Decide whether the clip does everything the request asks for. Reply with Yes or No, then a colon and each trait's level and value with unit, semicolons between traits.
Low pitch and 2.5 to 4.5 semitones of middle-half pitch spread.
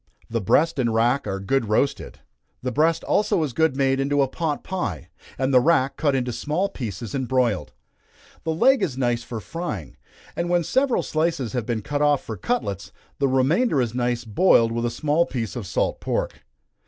No: low, 130 Hz; average, 5.2 semitones